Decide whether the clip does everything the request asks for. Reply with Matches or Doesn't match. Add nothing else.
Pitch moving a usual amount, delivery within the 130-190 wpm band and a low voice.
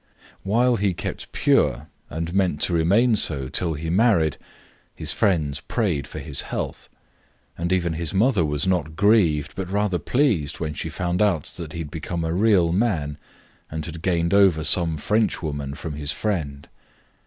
Matches